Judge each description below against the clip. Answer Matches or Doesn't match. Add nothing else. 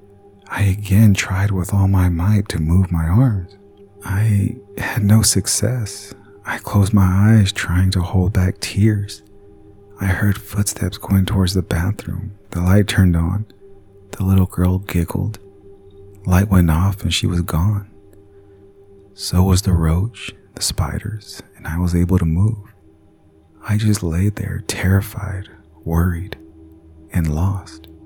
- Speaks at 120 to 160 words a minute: Matches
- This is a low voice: Matches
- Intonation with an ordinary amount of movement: Doesn't match